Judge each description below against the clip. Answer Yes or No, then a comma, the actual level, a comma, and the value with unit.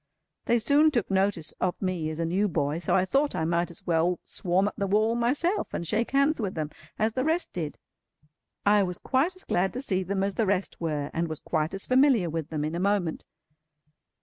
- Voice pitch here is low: No, high, 190 Hz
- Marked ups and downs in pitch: Yes, wide, 5.8 semitones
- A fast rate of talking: Yes, fast, 225 wpm